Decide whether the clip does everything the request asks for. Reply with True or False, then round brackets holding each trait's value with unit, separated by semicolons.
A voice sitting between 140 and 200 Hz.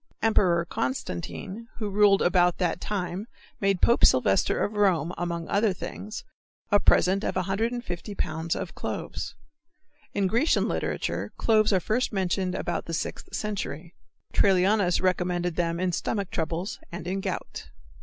True (185 Hz)